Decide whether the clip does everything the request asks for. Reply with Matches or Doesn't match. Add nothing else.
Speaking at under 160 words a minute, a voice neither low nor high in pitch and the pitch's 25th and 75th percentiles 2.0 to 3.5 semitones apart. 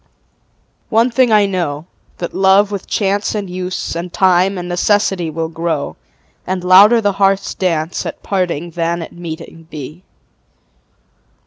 Matches